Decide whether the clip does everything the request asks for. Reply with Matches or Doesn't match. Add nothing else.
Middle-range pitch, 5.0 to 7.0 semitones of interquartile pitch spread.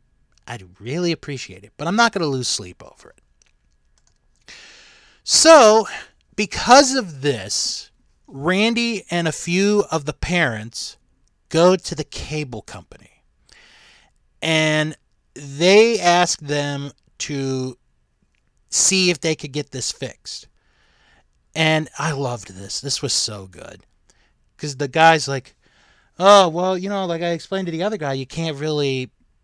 Matches